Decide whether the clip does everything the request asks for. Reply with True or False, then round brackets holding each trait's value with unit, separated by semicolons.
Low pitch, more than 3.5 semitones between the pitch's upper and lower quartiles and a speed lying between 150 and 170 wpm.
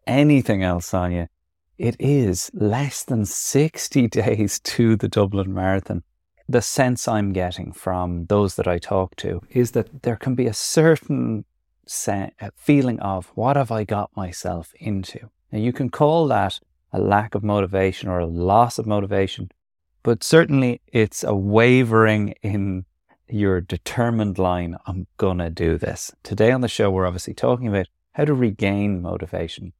True (105 Hz; 4.5 semitones; 155 wpm)